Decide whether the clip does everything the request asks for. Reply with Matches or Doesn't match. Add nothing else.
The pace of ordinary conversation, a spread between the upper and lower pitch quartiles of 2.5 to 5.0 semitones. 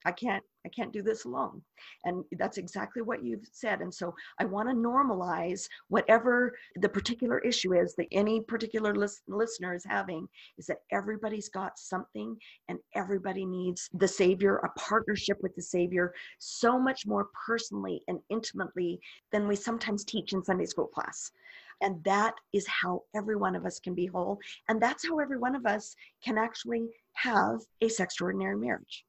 Matches